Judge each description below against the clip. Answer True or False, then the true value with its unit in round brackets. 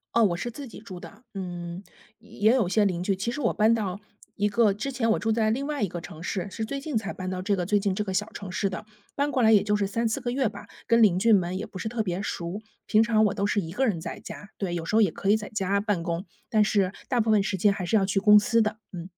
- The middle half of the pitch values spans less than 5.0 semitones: True (3.0 semitones)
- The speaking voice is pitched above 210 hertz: False (205 Hz)